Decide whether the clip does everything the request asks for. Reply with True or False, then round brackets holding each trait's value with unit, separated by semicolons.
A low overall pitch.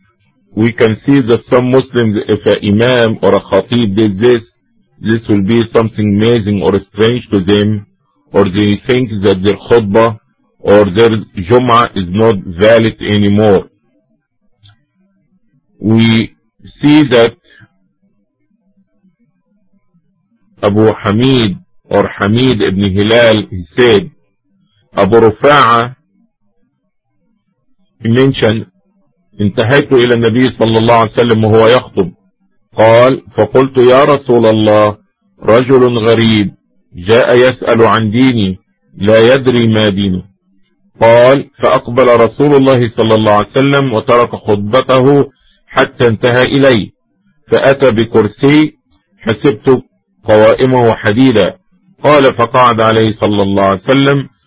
True (115 Hz)